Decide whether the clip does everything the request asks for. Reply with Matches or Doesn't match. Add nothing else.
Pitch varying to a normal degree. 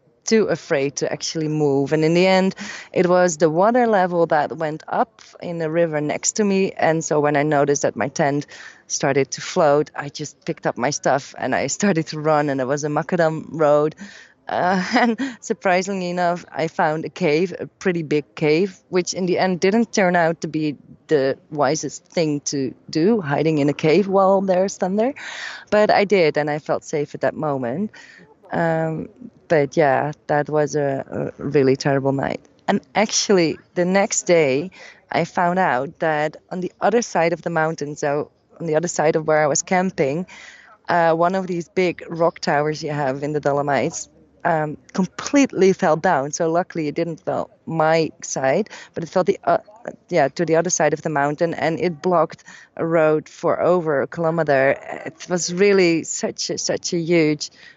Matches